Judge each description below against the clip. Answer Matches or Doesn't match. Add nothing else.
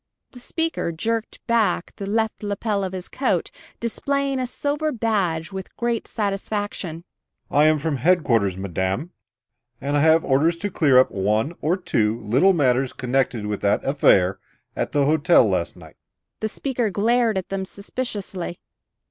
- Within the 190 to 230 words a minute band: Doesn't match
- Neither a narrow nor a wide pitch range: Doesn't match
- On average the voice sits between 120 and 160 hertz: Doesn't match